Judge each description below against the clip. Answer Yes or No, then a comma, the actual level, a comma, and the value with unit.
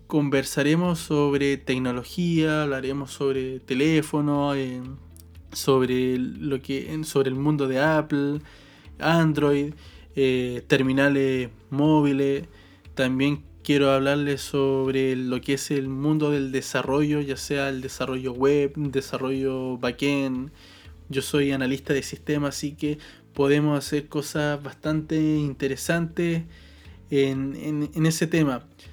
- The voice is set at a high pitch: No, medium, 140 Hz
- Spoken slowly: Yes, slow, 110 wpm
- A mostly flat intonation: Yes, narrow, 2.1 semitones